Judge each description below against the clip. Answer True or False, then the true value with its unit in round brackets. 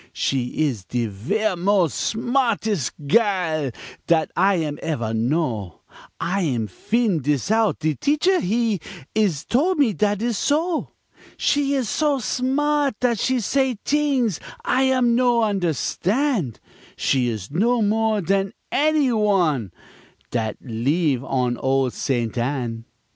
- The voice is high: True (195 Hz)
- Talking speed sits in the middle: False (130 wpm)